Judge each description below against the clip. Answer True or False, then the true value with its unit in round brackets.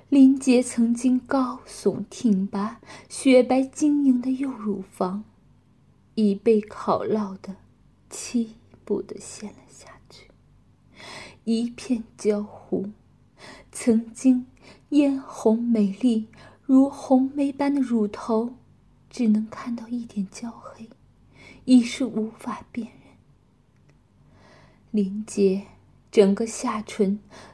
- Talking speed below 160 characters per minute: True (140 characters per minute)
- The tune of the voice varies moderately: True (3.5 semitones)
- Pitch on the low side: False (230 Hz)